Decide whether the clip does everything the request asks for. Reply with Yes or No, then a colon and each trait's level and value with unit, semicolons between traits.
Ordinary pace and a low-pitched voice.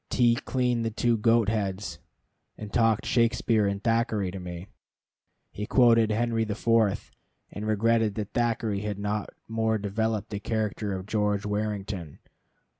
Yes: average, 145 wpm; low, 110 Hz